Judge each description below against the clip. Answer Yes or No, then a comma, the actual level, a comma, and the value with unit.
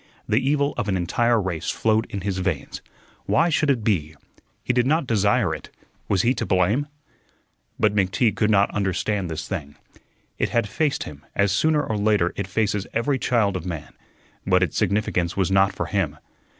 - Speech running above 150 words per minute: Yes, average, 185 wpm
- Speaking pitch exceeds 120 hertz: No, low, 100 Hz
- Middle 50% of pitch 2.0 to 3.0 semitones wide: No, average, 4.2 semitones